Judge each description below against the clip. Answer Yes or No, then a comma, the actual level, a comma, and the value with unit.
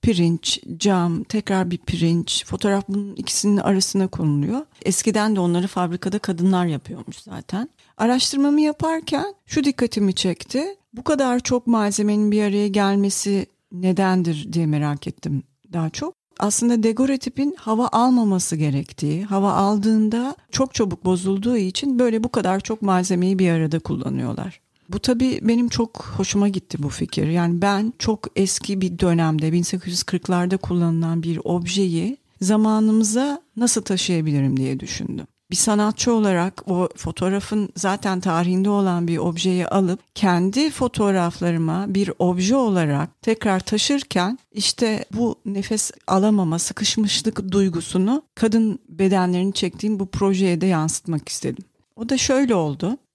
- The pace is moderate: Yes, average, 130 wpm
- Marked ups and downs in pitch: No, average, 3.9 semitones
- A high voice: Yes, high, 195 Hz